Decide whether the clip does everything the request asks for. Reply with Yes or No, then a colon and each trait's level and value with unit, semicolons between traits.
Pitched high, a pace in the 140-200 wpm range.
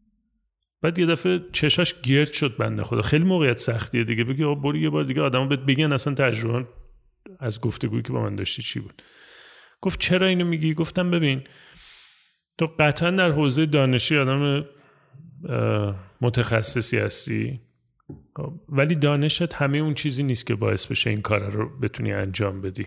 No: medium, 140 Hz; fast, 155 wpm